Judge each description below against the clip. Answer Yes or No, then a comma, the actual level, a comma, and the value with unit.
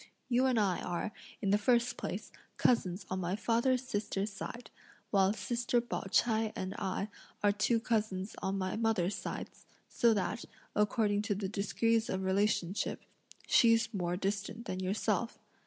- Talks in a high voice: Yes, high, 210 Hz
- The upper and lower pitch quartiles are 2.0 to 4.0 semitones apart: Yes, average, 3.1 semitones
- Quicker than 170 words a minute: No, average, 150 wpm